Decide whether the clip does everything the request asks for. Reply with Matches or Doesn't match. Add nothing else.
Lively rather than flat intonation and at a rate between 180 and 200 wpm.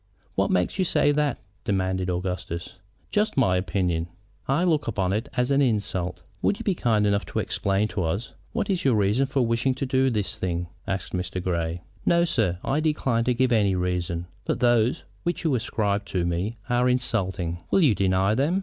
Matches